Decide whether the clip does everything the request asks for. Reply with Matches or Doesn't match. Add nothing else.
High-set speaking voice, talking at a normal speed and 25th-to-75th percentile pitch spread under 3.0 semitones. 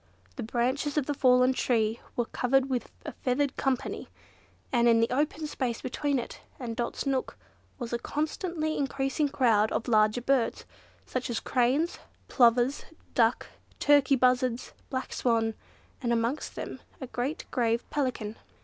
Matches